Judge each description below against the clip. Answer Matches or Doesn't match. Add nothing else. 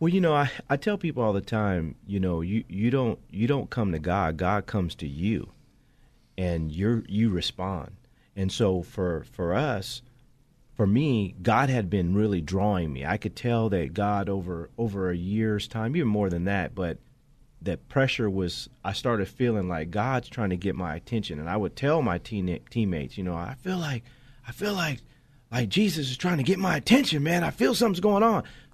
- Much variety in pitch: Matches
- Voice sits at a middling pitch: Doesn't match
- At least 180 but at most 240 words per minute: Matches